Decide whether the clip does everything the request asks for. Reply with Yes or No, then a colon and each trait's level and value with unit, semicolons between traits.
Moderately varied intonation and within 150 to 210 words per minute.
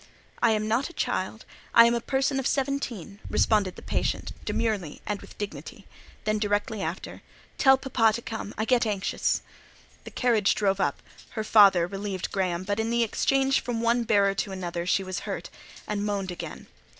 Yes: average, 3.1 semitones; average, 175 wpm